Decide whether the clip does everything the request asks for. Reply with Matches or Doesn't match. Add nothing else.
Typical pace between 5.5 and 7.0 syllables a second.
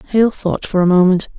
Matches